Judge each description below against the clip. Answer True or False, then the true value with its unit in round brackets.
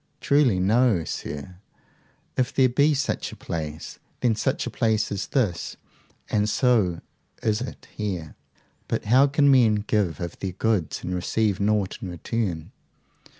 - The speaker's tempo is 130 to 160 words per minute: True (150 wpm)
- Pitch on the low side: True (105 Hz)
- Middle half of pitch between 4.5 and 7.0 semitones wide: True (5.4 semitones)